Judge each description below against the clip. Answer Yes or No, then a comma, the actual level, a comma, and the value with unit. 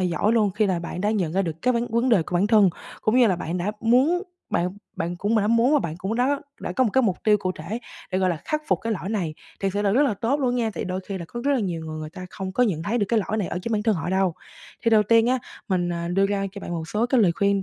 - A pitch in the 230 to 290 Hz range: No, high, 205 Hz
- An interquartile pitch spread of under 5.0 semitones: Yes, average, 4.2 semitones